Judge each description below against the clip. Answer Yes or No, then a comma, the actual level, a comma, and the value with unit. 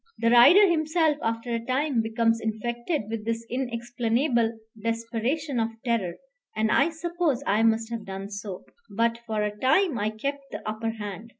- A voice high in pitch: Yes, high, 230 Hz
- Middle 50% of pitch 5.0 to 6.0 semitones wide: No, average, 3.2 semitones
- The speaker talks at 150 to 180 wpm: Yes, average, 165 wpm